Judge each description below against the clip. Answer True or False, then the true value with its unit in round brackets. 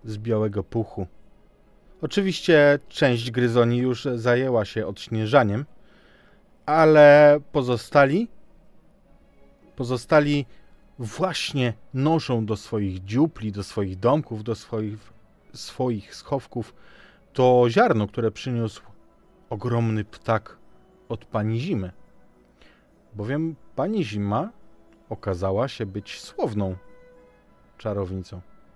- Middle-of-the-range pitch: False (115 Hz)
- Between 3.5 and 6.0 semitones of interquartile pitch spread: True (4.7 semitones)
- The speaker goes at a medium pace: False (90 wpm)